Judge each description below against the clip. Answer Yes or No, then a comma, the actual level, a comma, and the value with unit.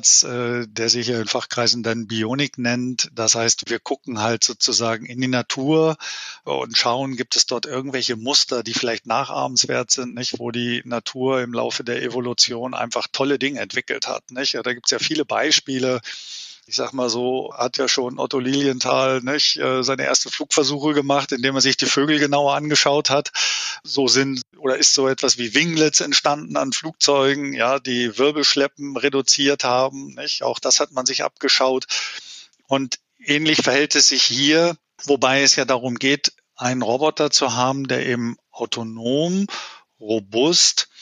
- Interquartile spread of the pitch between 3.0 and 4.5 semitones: No, narrow, 2.4 semitones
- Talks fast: No, average, 165 wpm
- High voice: No, low, 130 Hz